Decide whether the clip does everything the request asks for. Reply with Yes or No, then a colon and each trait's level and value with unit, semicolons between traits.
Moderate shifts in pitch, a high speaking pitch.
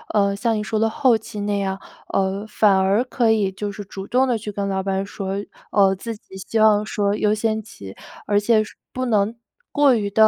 No: narrow, 2.0 semitones; high, 210 Hz